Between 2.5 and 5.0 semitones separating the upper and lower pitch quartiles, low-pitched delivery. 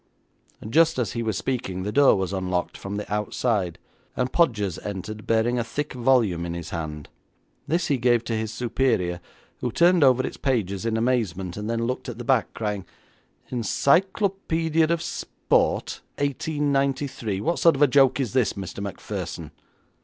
No: wide, 5.6 semitones; low, 115 Hz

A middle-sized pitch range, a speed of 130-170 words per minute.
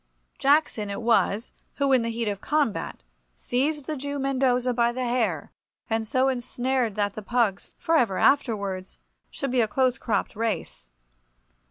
Yes: average, 3.7 semitones; average, 160 wpm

